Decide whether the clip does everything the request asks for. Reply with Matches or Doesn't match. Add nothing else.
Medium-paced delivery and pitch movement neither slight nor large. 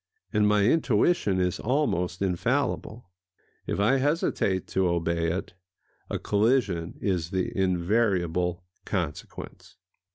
Doesn't match